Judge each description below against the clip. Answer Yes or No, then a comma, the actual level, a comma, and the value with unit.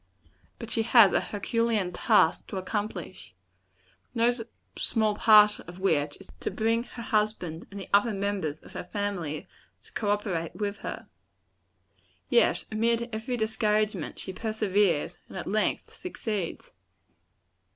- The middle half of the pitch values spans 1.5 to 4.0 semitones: Yes, average, 2.8 semitones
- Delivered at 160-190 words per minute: No, slow, 135 wpm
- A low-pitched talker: No, high, 210 Hz